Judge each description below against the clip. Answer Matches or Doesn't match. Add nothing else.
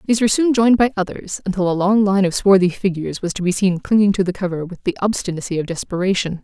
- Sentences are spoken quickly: Matches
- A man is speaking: Doesn't match